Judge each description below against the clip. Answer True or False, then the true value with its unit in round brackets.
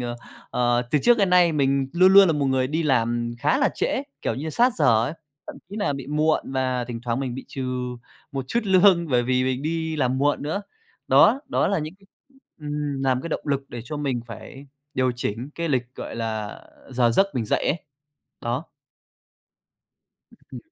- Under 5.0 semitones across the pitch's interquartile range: True (4.4 semitones)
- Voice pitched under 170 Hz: True (135 Hz)